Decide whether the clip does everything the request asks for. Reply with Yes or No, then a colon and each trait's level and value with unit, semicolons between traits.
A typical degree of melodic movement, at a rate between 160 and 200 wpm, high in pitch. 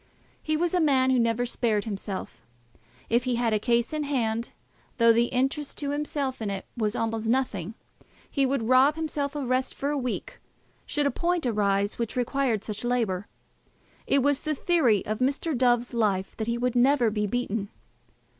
Yes: average, 3.9 semitones; average, 185 wpm; high, 245 Hz